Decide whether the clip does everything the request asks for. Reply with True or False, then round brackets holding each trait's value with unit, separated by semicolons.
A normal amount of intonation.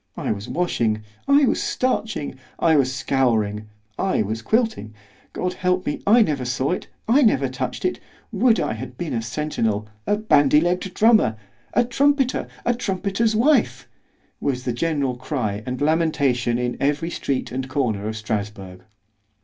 False (8.8 semitones)